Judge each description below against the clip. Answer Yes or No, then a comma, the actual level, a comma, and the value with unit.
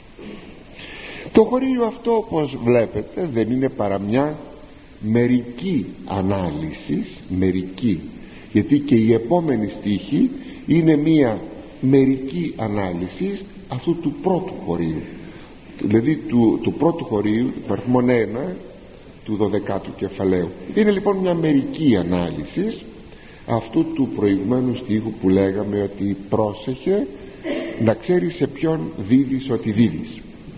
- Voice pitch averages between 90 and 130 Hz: Yes, low, 125 Hz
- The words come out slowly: Yes, slow, 110 wpm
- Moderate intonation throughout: No, wide, 7.4 semitones